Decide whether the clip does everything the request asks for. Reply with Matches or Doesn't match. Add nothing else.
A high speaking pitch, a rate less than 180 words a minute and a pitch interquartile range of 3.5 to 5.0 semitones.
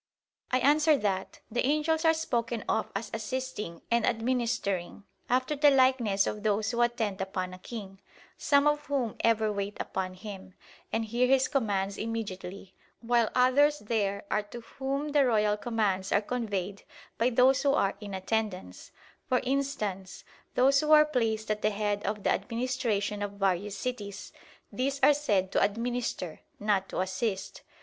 Matches